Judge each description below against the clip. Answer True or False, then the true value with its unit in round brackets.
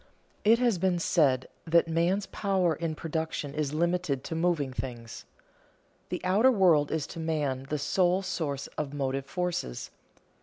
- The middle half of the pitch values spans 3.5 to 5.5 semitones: True (4.1 semitones)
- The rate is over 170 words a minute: False (155 wpm)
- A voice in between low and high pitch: True (160 Hz)